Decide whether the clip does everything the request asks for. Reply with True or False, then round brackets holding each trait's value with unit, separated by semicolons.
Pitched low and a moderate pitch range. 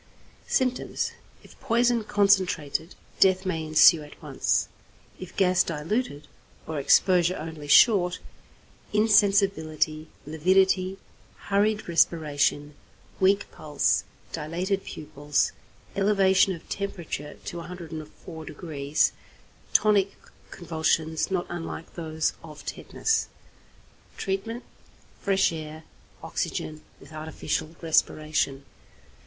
False (170 Hz; 3.9 semitones)